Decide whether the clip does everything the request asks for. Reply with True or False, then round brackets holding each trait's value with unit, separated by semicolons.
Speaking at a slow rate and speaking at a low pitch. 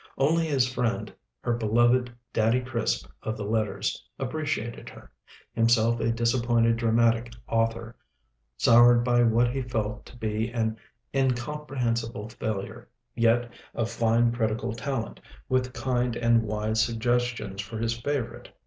True (130 wpm; 115 Hz)